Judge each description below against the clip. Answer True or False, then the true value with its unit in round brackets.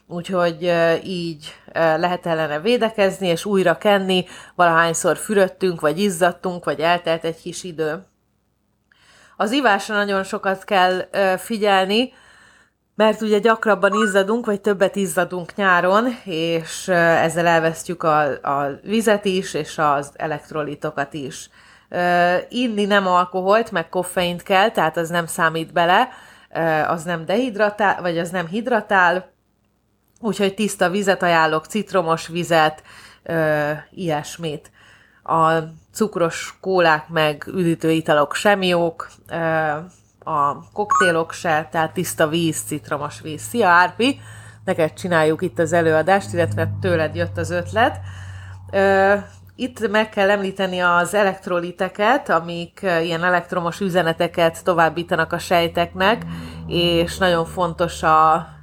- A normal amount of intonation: True (3.3 semitones)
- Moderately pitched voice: True (175 Hz)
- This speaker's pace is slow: False (115 wpm)